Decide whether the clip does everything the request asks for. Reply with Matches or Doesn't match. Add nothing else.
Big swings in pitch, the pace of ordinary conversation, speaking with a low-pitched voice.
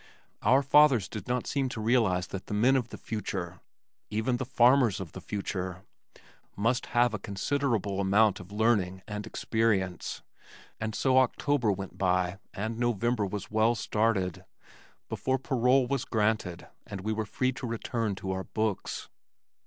Doesn't match